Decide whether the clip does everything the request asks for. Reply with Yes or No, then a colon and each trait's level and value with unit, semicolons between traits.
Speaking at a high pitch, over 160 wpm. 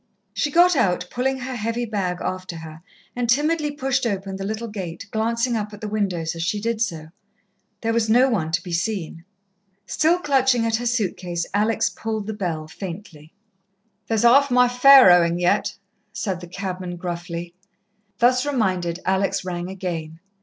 Yes: high, 205 Hz; average, 170 wpm